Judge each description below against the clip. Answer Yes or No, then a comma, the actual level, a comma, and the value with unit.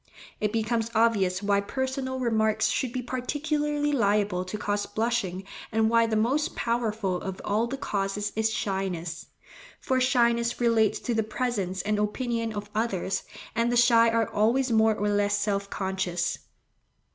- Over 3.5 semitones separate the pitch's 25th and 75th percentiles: No, average, 2.7 semitones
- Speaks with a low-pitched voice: No, high, 220 Hz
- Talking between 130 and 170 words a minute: Yes, average, 155 wpm